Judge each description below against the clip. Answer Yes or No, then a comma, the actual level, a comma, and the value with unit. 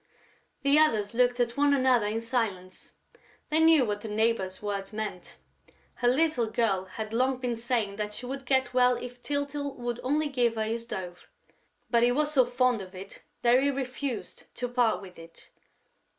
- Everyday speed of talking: Yes, average, 180 wpm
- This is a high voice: Yes, high, 240 Hz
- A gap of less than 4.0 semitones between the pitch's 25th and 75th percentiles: Yes, average, 3.4 semitones